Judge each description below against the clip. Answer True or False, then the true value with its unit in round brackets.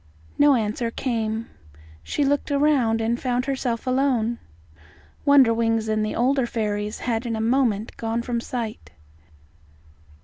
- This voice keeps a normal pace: False (130 wpm)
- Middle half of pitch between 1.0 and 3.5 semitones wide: True (2.7 semitones)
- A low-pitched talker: False (235 Hz)